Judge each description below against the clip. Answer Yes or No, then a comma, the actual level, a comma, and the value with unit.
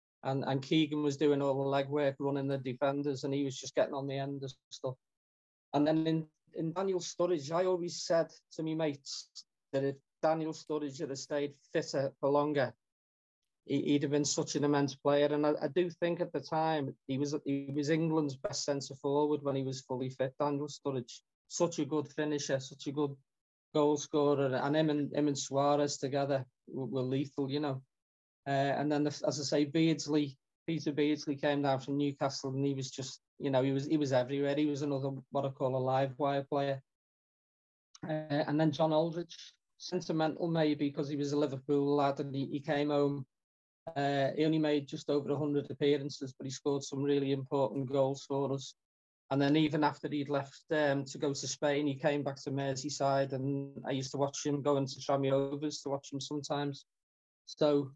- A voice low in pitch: No, medium, 145 Hz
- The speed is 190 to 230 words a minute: Yes, average, 200 wpm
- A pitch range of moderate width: No, narrow, 1.6 semitones